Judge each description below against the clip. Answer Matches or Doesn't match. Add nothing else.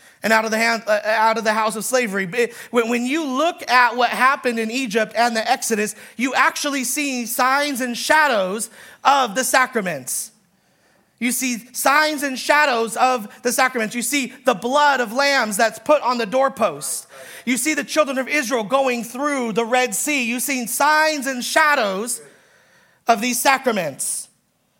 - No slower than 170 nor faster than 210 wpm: Doesn't match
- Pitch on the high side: Matches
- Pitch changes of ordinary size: Matches